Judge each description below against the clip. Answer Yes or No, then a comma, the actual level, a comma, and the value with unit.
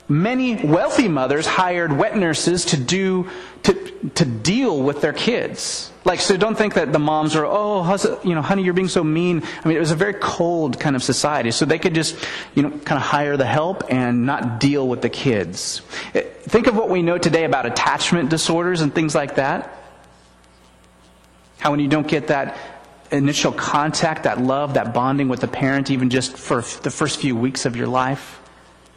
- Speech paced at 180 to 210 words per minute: Yes, average, 200 wpm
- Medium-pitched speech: Yes, medium, 150 Hz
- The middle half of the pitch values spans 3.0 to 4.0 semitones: No, average, 4.6 semitones